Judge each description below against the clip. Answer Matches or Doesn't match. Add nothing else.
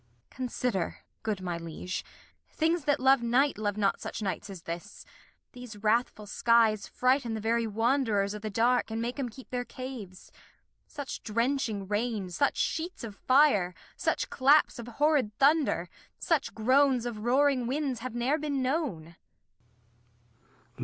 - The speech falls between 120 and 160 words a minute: Matches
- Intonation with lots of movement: Doesn't match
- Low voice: Doesn't match